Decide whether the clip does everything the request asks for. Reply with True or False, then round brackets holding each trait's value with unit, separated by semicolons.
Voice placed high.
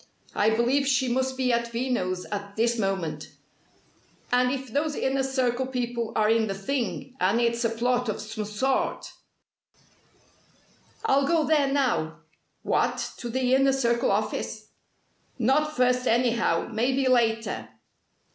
True (245 Hz)